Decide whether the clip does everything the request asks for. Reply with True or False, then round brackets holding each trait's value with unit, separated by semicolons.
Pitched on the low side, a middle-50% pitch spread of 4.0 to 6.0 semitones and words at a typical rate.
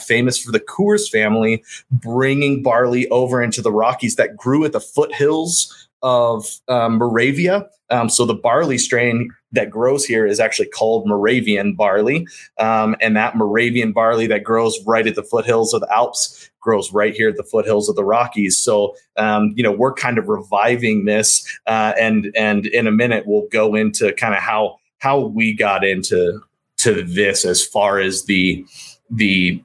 False (115 Hz; 3.6 semitones; 175 wpm)